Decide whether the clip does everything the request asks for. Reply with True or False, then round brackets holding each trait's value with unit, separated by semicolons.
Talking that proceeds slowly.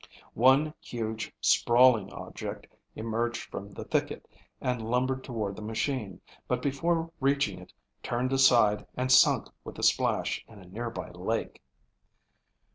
True (130 wpm)